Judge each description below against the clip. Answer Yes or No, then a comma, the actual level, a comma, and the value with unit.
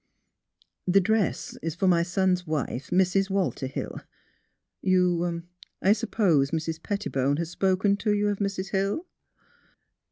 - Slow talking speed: Yes, slow, 125 wpm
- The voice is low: No, medium, 185 Hz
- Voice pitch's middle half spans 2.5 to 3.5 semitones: Yes, average, 2.9 semitones